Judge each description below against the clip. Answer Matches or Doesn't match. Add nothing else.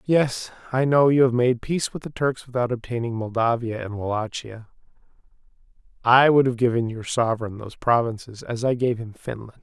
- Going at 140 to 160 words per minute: Doesn't match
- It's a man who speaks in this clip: Matches